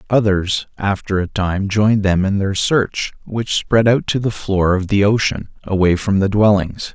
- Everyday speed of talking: Yes, average, 190 wpm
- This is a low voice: Yes, low, 100 Hz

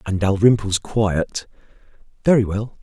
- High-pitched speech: No, low, 105 Hz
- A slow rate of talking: Yes, slow, 105 wpm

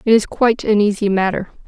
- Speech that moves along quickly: Yes, fast, 215 wpm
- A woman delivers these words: Yes, female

